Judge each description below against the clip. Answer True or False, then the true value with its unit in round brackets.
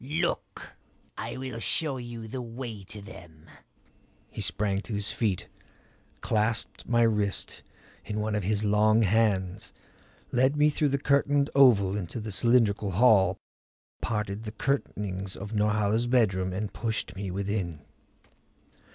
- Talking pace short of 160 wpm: True (135 wpm)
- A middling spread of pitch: True (3.2 semitones)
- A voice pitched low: True (105 Hz)